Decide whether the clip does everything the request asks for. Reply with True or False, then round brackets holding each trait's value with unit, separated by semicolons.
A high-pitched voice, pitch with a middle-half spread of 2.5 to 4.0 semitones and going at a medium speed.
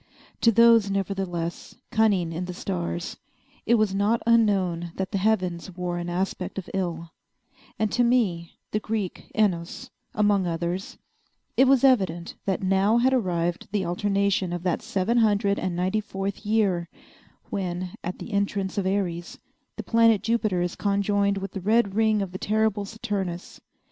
True (195 Hz; 3.3 semitones; 160 wpm)